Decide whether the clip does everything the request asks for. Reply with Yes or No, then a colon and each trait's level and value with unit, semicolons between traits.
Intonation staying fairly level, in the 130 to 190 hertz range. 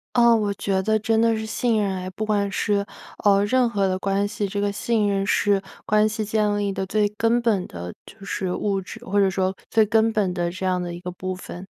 No: narrow, 2.2 semitones; high, 205 Hz